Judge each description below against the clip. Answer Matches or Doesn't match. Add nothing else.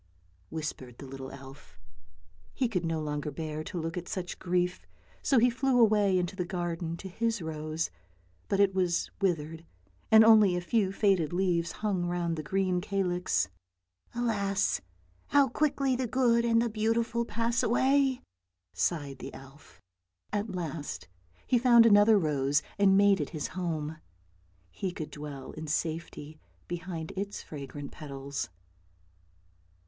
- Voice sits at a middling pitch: Matches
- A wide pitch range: Matches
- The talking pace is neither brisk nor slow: Matches